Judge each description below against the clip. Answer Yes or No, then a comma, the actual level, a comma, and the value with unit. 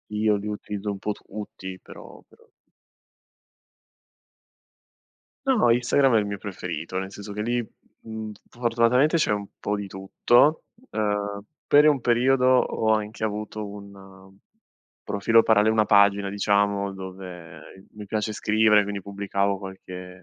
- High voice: No, low, 105 Hz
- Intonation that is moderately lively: No, narrow, 2.0 semitones